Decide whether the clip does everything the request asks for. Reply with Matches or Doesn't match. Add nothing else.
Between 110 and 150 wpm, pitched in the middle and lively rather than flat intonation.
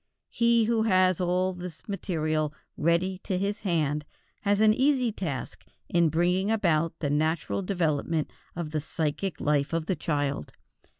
Doesn't match